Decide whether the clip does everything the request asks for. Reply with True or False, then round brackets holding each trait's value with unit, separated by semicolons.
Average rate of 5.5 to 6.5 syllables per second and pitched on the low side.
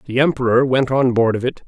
True (6.0 syllables/s; 125 Hz)